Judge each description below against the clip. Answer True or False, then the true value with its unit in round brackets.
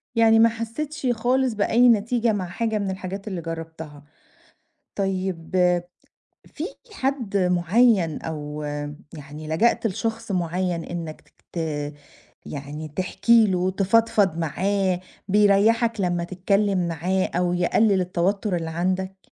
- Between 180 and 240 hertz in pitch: True (190 Hz)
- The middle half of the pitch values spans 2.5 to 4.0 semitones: False (4.5 semitones)